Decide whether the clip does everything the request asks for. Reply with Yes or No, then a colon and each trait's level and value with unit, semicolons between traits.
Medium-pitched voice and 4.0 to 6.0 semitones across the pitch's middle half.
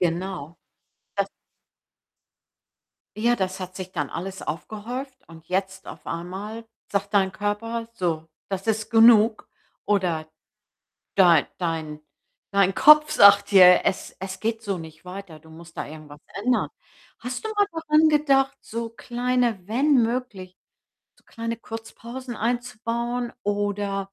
No: high, 205 Hz; average, 4.3 semitones